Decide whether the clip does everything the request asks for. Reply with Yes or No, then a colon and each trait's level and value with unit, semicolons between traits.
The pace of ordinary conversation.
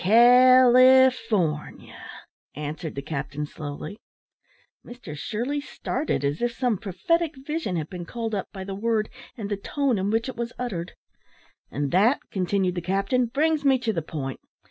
Yes: average, 155 wpm